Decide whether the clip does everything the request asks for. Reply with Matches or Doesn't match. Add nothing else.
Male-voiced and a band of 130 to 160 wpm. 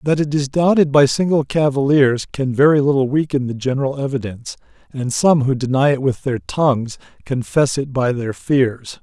Doesn't match